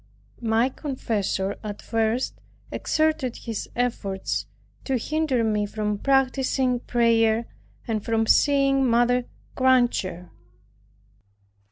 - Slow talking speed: Yes, slow, 90 wpm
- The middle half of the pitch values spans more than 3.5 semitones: No, average, 3.1 semitones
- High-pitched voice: Yes, high, 235 Hz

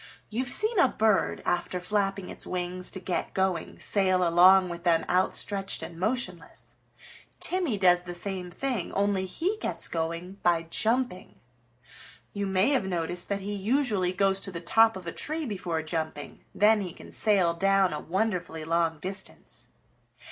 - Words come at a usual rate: Yes, average, 160 wpm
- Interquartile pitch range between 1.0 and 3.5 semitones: Yes, average, 2.9 semitones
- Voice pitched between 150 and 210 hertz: Yes, high, 190 Hz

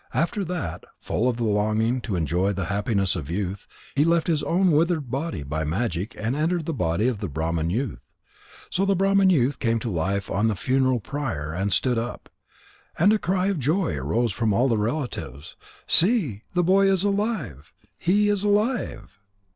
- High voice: No, low, 120 Hz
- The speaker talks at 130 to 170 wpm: No, average, 185 wpm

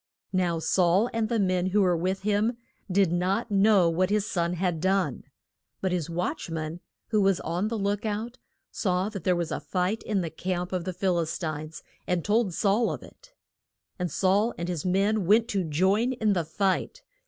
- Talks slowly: No, average, 200 wpm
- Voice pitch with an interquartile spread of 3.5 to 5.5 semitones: No, average, 3.0 semitones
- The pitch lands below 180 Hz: No, medium, 185 Hz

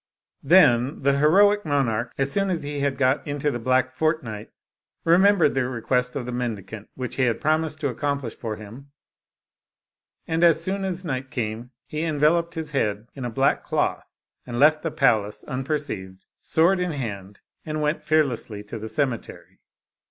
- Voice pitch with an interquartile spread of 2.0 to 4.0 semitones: No, average, 4.8 semitones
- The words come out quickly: No, average, 170 wpm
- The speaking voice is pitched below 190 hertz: Yes, medium, 140 Hz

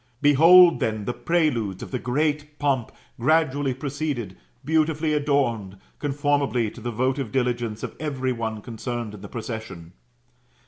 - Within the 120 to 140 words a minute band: Yes, slow, 135 wpm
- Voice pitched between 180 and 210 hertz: No, low, 130 Hz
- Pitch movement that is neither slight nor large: Yes, average, 4.4 semitones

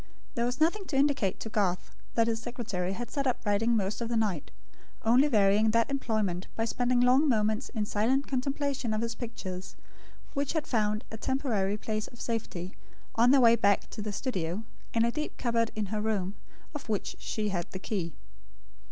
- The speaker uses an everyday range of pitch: Yes, average, 3.3 semitones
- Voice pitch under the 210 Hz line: No, high, 225 Hz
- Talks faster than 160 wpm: Yes, average, 190 wpm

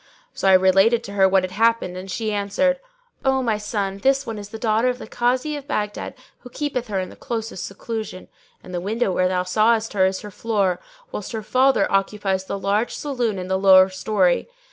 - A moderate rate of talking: No, fast, 215 wpm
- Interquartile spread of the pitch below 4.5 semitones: Yes, average, 3.5 semitones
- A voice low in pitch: No, high, 210 Hz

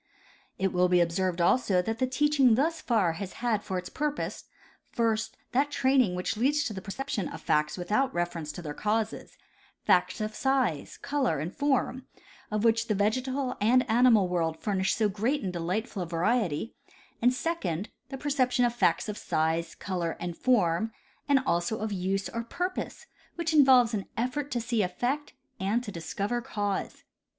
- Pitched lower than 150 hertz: No, high, 220 Hz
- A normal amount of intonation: No, wide, 5.9 semitones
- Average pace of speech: Yes, average, 175 wpm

